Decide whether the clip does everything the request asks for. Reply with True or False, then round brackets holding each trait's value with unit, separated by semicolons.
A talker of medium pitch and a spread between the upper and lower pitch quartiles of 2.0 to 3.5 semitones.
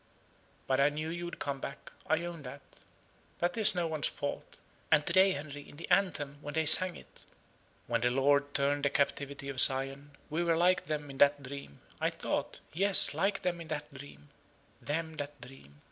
True (145 Hz; 3.0 semitones)